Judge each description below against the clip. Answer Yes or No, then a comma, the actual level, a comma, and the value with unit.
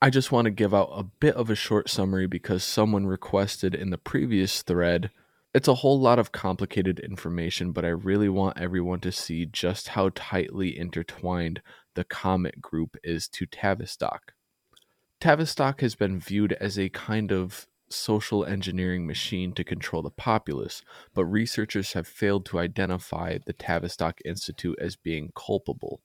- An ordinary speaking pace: Yes, average, 160 wpm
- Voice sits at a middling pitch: No, very low, 95 Hz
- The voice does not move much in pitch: No, average, 3.1 semitones